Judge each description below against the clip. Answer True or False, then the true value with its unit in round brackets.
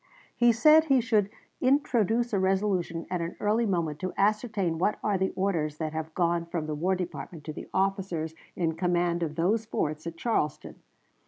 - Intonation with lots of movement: False (4.3 semitones)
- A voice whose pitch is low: False (185 Hz)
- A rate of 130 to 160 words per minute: False (180 wpm)